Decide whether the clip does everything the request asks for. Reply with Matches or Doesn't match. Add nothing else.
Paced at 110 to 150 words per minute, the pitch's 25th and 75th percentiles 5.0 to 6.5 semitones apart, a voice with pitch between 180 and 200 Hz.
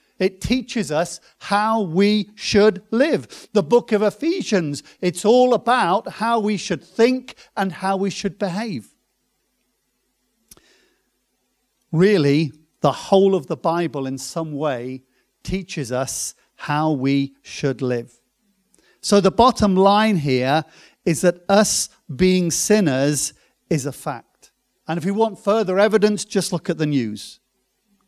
Matches